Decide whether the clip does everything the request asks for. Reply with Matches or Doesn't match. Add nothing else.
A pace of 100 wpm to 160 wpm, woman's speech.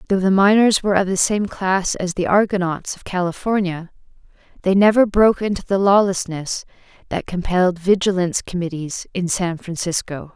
Matches